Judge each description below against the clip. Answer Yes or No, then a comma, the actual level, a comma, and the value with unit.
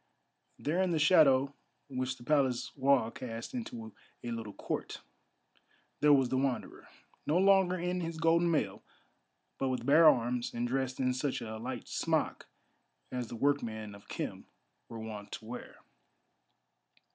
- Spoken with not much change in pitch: No, average, 4.4 semitones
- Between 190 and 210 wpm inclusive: No, average, 150 wpm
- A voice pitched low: Yes, low, 130 Hz